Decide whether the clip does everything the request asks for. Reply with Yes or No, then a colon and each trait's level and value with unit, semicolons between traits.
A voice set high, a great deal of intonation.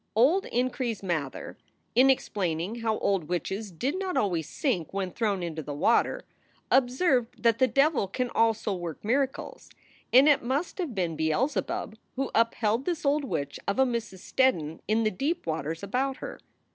Yes: high, 230 Hz; wide, 6.6 semitones